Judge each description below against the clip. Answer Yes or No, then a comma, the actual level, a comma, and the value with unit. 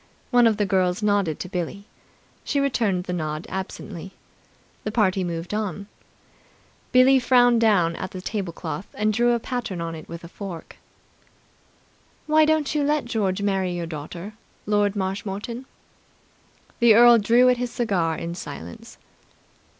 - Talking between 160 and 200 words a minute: No, average, 150 wpm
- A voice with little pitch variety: No, average, 4.9 semitones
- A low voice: No, high, 200 Hz